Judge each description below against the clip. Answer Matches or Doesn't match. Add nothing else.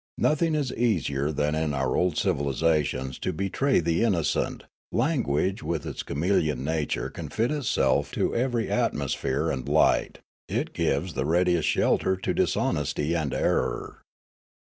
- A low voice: Matches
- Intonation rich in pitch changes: Matches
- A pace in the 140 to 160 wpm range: Matches